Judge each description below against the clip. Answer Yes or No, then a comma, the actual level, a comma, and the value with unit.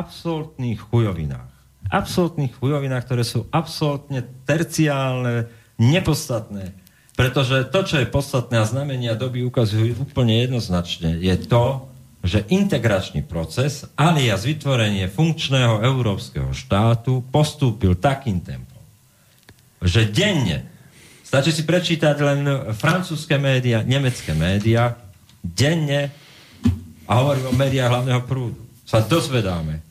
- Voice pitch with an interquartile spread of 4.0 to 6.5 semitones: Yes, average, 4.4 semitones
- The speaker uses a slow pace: Yes, slow, 105 wpm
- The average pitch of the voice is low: Yes, low, 125 Hz